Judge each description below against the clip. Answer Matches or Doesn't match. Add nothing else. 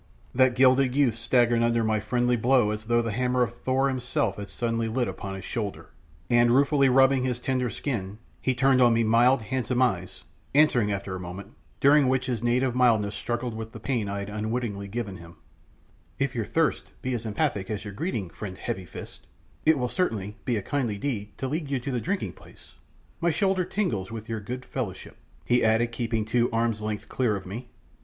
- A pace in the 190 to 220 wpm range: Matches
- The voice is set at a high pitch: Doesn't match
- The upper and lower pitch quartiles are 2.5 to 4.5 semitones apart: Matches